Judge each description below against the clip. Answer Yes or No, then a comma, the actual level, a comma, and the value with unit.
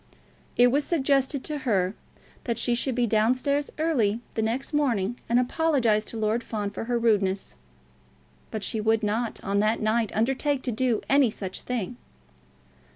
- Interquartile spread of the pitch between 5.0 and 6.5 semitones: No, average, 3.6 semitones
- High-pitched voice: Yes, high, 235 Hz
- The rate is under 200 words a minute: Yes, average, 165 wpm